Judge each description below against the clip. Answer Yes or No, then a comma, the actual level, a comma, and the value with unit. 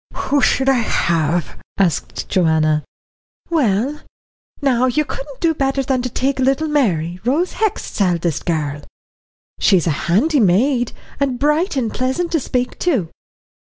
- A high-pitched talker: Yes, very high, 250 Hz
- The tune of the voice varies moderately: No, wide, 8.2 semitones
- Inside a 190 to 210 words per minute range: No, slow, 135 wpm